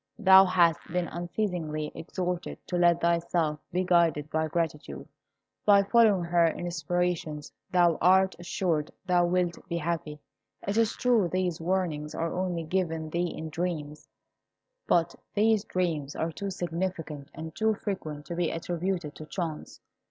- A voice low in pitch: No, medium, 170 Hz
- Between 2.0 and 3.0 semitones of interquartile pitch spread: Yes, narrow, 2.4 semitones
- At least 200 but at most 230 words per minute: No, average, 145 wpm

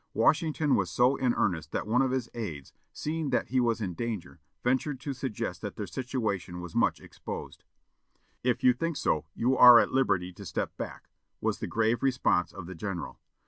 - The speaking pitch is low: Yes, low, 120 Hz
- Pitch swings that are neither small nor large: No, wide, 5.8 semitones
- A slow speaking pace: No, average, 190 wpm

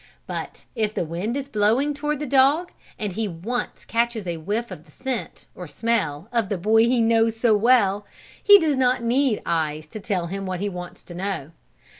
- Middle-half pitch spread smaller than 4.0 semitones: No, average, 5.1 semitones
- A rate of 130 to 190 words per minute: No, average, 200 wpm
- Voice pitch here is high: Yes, high, 220 Hz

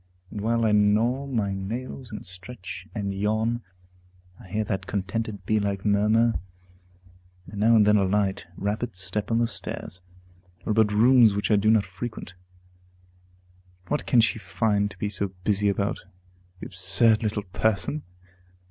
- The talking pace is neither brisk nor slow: Yes, average, 155 wpm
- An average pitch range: No, narrow, 2.2 semitones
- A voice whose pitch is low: Yes, low, 105 Hz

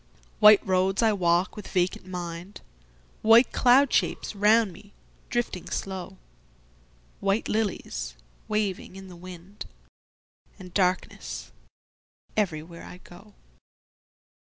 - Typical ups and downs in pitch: Yes, average, 3.5 semitones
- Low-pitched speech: No, medium, 185 Hz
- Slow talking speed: Yes, slow, 90 wpm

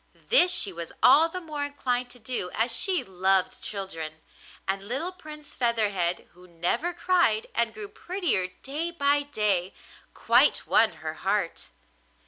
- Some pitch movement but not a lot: No, wide, 8.0 semitones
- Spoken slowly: No, average, 145 wpm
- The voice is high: Yes, high, 235 Hz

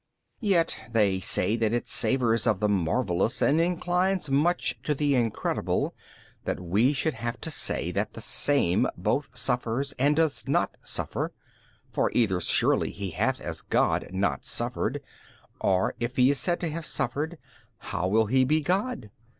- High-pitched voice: No, low, 125 Hz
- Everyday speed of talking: Yes, average, 165 wpm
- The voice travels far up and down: Yes, wide, 6.9 semitones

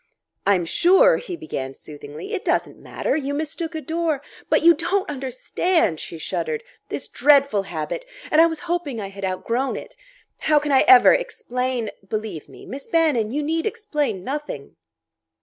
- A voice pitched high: Yes, very high, 290 Hz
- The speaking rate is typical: Yes, average, 170 wpm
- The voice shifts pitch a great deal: Yes, wide, 7.7 semitones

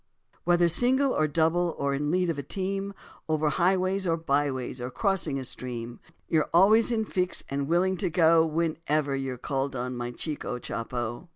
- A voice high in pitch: No, medium, 160 Hz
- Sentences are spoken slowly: No, average, 180 wpm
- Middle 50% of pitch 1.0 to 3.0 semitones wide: No, average, 5.0 semitones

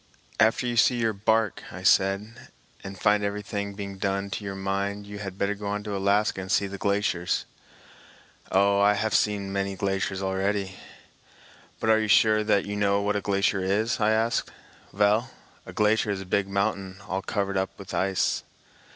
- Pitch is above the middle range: No, low, 100 Hz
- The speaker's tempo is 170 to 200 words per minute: Yes, average, 185 wpm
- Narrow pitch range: Yes, narrow, 1.3 semitones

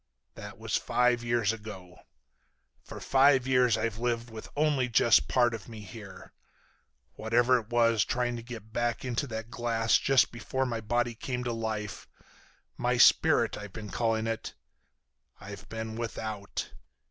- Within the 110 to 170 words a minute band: Yes, average, 145 wpm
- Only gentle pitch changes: Yes, narrow, 1.8 semitones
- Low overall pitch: Yes, low, 115 Hz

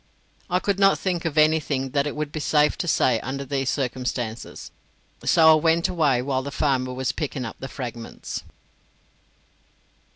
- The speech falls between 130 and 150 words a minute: No, average, 165 wpm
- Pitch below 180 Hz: Yes, medium, 140 Hz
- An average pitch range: Yes, average, 3.4 semitones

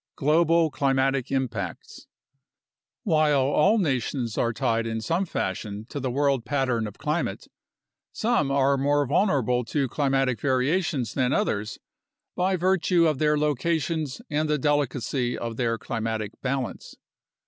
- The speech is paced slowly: Yes, slow, 130 wpm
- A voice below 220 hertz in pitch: Yes, low, 135 Hz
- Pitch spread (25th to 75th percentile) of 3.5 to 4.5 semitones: Yes, average, 3.9 semitones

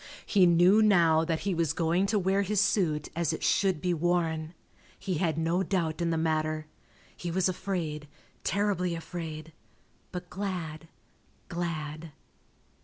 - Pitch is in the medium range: Yes, medium, 170 Hz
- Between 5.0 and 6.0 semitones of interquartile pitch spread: No, average, 2.8 semitones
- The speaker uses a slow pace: No, average, 145 wpm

